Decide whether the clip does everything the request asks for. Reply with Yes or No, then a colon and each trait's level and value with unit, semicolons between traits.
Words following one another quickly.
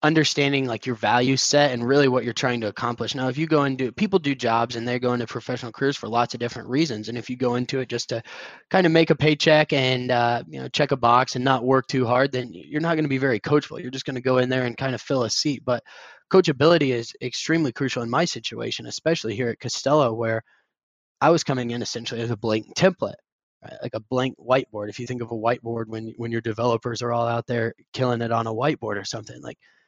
Yes: fast, 255 wpm